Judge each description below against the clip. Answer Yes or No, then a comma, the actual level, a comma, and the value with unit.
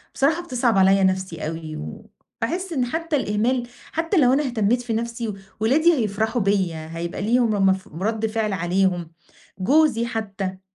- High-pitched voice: Yes, high, 220 Hz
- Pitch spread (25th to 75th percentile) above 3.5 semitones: Yes, average, 4.8 semitones